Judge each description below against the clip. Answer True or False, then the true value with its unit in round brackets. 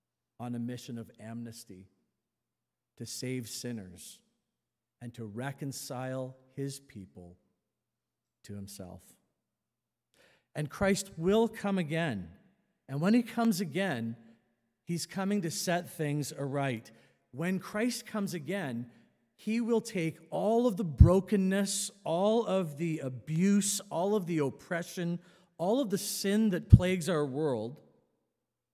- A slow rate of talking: True (120 wpm)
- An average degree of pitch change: False (8.4 semitones)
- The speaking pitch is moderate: True (160 Hz)